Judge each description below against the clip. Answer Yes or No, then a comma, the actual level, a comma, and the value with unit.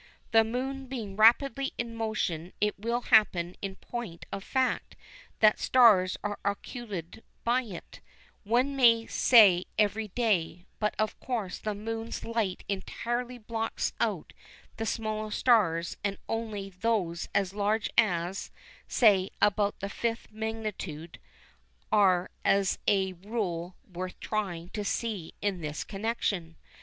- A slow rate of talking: Yes, slow, 130 wpm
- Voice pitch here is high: Yes, high, 210 Hz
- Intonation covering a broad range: No, average, 3.4 semitones